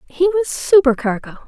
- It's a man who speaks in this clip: No, female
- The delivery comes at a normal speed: No, slow, 120 wpm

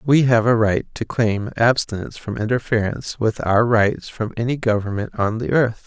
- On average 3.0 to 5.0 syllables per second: Yes, 4.9 syllables/s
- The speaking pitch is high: No, low, 115 Hz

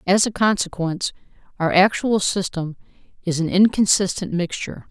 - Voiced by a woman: Yes, female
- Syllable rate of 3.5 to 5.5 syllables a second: Yes, 5.2 syllables/s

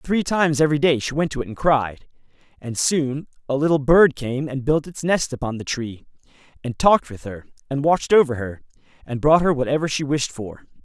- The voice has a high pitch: No, medium, 140 Hz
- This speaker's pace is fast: Yes, fast, 210 wpm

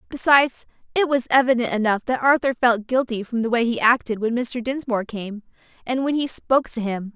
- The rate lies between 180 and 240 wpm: Yes, average, 200 wpm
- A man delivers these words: No, female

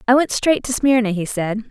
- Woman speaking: Yes, female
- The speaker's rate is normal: No, fast, 245 wpm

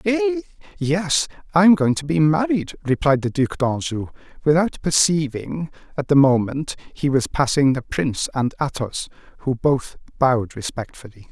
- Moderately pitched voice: Yes, medium, 145 Hz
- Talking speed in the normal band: Yes, average, 150 wpm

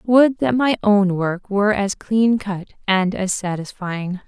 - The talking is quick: No, average, 170 wpm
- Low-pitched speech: No, high, 205 Hz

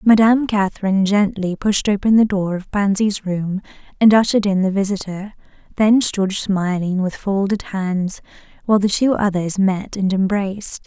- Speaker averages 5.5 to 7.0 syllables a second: No, 4.9 syllables/s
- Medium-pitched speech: No, high, 200 Hz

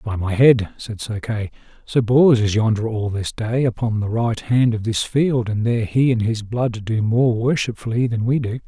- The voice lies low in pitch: Yes, low, 115 Hz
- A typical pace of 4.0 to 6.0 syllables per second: Yes, 4.7 syllables/s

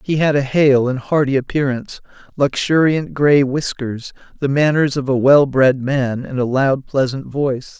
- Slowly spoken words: No, average, 170 wpm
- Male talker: Yes, male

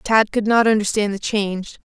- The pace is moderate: Yes, average, 190 wpm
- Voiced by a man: No, female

